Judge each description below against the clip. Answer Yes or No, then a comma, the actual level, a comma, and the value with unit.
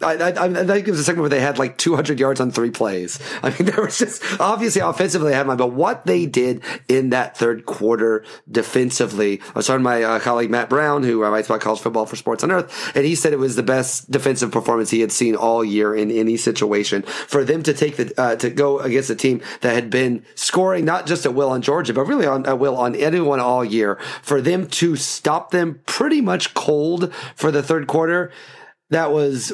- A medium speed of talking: No, fast, 235 wpm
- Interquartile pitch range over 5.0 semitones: Yes, wide, 5.5 semitones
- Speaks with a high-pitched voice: No, low, 135 Hz